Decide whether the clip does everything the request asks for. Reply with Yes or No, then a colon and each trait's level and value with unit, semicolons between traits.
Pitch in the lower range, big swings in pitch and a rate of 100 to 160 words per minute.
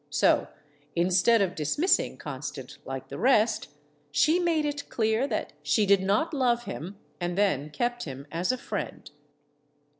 No: high, 200 Hz; wide, 8.2 semitones; average, 155 wpm